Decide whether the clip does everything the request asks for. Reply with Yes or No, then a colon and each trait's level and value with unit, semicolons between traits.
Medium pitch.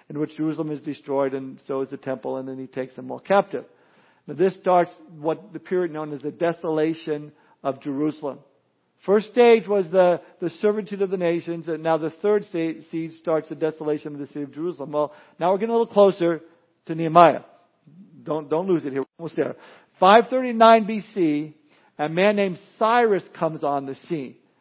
Yes: medium, 165 Hz